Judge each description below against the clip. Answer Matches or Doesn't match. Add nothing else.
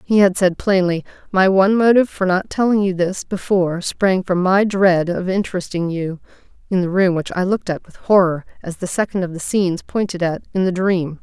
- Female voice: Matches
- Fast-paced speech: Matches